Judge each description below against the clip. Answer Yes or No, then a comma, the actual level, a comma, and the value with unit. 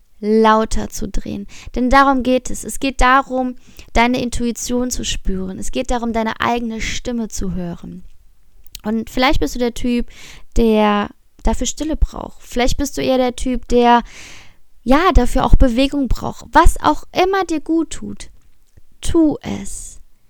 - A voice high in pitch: Yes, high, 245 Hz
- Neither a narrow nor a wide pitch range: Yes, average, 3.2 semitones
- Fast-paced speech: No, average, 155 wpm